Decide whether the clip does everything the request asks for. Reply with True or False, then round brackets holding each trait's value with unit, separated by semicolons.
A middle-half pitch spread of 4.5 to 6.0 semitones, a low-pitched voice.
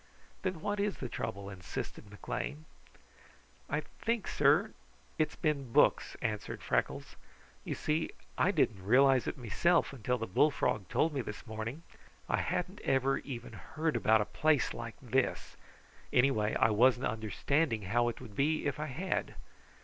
True (5.6 semitones; 130 Hz)